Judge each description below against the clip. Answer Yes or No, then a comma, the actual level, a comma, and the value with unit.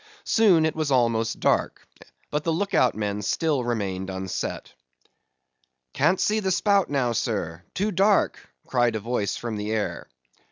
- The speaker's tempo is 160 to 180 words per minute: No, average, 145 wpm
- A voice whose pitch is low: Yes, low, 125 Hz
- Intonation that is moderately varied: No, wide, 7.7 semitones